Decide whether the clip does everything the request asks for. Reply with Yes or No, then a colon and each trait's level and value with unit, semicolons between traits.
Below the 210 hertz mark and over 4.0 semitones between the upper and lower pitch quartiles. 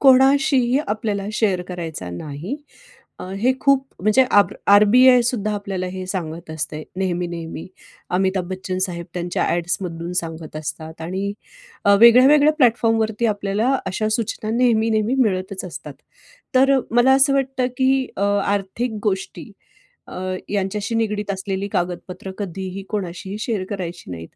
Yes: high, 200 Hz; average, 4.7 semitones